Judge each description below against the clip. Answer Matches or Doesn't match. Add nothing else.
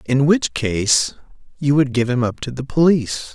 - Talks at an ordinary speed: Matches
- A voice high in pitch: Doesn't match